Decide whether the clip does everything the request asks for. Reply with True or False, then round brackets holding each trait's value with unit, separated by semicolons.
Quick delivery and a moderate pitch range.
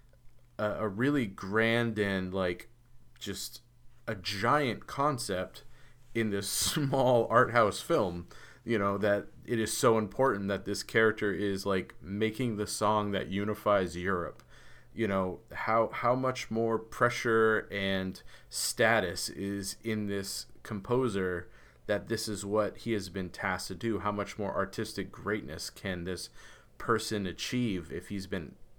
False (140 wpm; 3.0 semitones)